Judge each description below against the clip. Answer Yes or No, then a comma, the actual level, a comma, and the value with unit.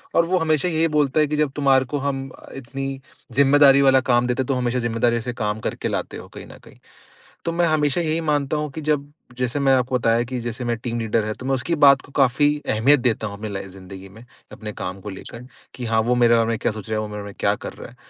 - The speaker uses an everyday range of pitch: Yes, average, 4.0 semitones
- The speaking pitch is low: Yes, low, 130 Hz